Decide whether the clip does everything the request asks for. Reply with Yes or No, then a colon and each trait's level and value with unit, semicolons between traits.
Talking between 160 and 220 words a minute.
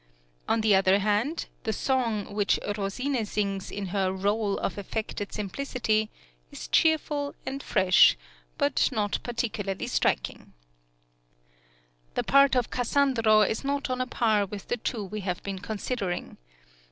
No: average, 140 wpm